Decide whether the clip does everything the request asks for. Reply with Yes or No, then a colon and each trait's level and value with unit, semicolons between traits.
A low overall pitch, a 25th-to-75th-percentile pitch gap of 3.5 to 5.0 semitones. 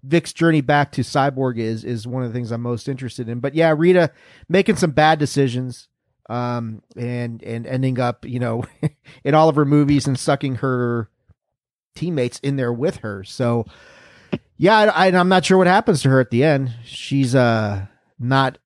Yes: low, 130 Hz; average, 4.1 semitones